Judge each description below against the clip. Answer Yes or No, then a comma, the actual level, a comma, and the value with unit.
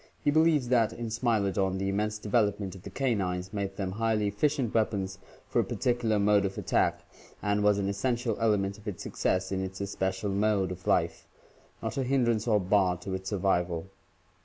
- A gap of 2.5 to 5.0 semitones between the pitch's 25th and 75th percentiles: Yes, average, 2.9 semitones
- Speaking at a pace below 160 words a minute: No, average, 185 wpm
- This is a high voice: No, low, 105 Hz